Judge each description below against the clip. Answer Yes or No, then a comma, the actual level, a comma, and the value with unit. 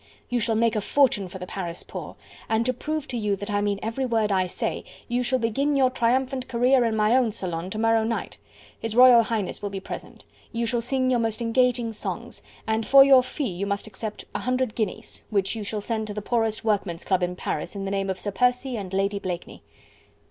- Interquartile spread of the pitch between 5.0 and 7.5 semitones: No, average, 3.7 semitones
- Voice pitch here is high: Yes, high, 225 Hz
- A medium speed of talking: No, fast, 230 wpm